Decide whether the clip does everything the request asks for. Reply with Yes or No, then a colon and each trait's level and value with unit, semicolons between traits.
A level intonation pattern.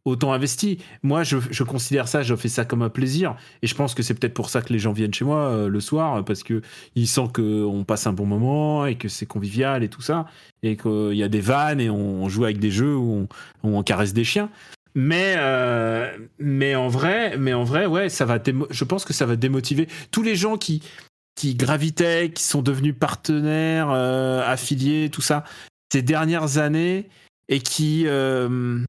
No: average, 4.7 semitones